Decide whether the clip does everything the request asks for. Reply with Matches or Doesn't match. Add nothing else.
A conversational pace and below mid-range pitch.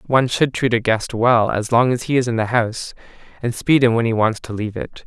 Doesn't match